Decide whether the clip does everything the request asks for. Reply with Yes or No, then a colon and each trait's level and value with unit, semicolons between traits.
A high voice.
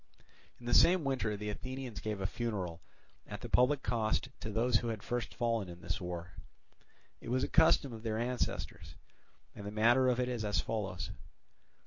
No: low, 115 Hz